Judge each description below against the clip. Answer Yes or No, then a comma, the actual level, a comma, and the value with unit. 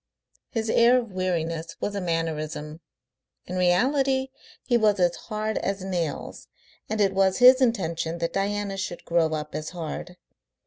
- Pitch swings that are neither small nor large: Yes, average, 4.5 semitones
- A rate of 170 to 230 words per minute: No, average, 150 wpm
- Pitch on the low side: No, medium, 185 Hz